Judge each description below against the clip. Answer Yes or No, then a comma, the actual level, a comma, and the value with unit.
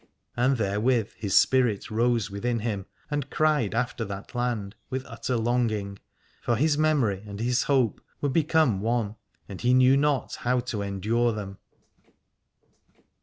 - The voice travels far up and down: No, average, 3.7 semitones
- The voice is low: Yes, low, 120 Hz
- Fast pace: No, average, 145 wpm